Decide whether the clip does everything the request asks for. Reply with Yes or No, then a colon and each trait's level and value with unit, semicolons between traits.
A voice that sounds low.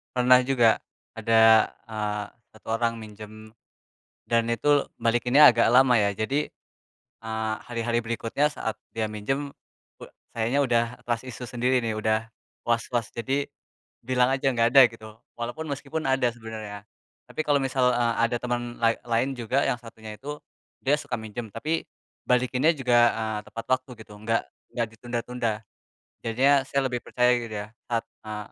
Yes: low, 120 Hz